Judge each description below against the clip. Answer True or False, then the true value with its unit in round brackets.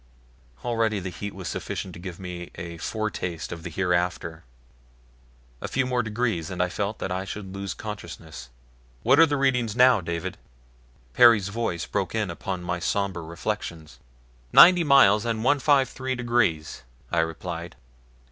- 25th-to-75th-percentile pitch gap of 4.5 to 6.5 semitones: True (5.2 semitones)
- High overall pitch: False (100 Hz)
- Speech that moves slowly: False (150 wpm)